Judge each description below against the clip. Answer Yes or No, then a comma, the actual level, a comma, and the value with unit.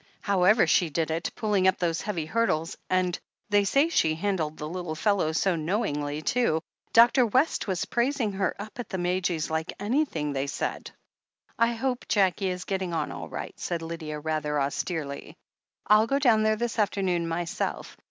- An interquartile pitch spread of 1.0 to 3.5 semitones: No, average, 5.2 semitones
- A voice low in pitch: No, medium, 185 Hz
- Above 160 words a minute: Yes, average, 180 wpm